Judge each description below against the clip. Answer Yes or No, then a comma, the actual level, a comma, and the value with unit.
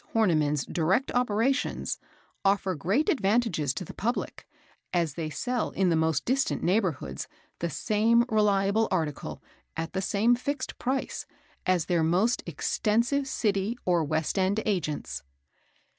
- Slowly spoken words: Yes, slow, 130 wpm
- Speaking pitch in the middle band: No, high, 195 Hz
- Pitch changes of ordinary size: No, wide, 5.9 semitones